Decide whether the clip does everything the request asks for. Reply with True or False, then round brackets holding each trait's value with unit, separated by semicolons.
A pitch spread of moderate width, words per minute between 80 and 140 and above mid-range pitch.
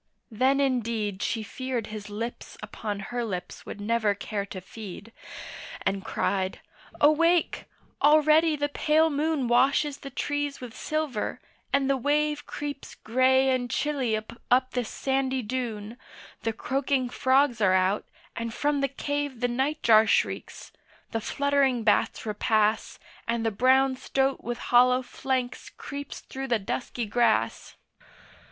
True (3.9 semitones; 135 wpm; 255 Hz)